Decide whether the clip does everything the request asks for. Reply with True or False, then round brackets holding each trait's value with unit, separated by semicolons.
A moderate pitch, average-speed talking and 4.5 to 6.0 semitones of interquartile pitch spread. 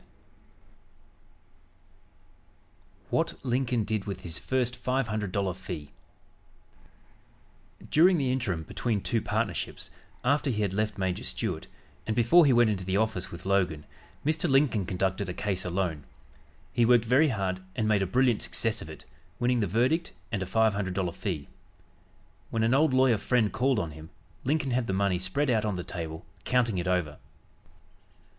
False (110 Hz; 165 wpm; 5.0 semitones)